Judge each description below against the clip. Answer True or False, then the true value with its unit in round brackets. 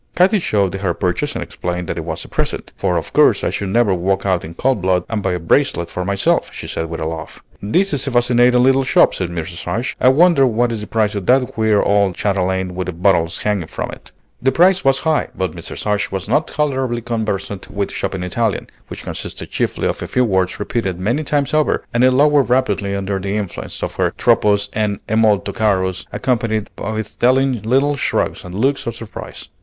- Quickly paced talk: True (215 wpm)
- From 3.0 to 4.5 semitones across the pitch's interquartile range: False (5.2 semitones)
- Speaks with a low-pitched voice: True (105 Hz)